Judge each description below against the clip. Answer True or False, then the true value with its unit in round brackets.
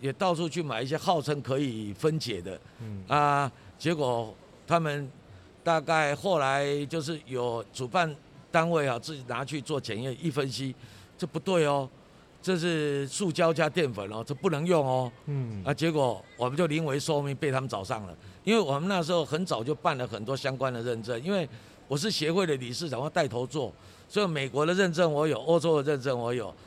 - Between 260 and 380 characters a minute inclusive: True (280 characters per minute)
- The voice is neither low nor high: True (145 Hz)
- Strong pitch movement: False (4.6 semitones)